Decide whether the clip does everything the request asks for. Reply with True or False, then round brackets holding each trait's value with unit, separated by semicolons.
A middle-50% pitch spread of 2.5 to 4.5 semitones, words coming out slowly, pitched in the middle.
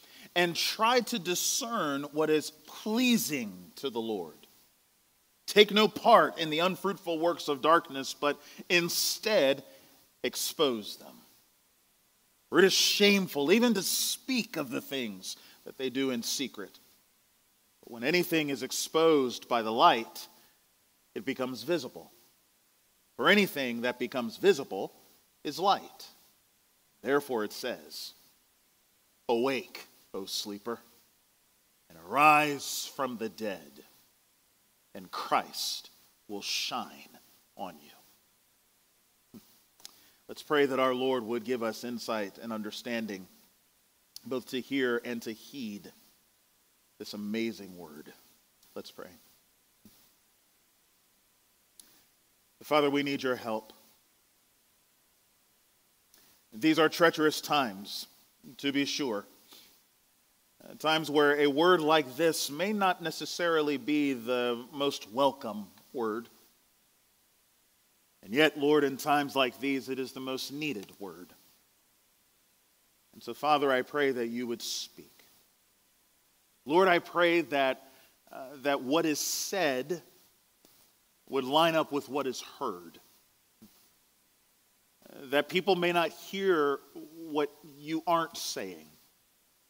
False (5.2 semitones; 115 wpm; 145 Hz)